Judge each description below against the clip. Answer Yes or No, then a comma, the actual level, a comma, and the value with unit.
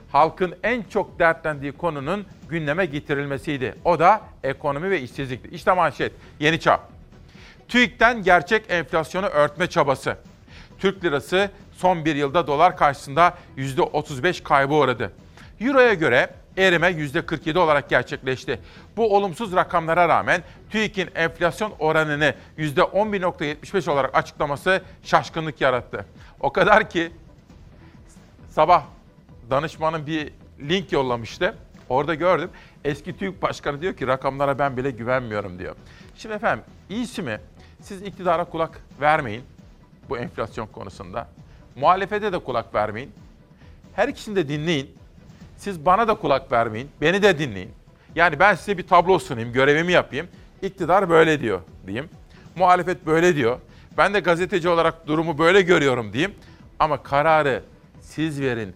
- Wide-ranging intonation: No, average, 4.7 semitones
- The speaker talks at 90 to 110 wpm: No, average, 125 wpm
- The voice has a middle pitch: Yes, medium, 165 Hz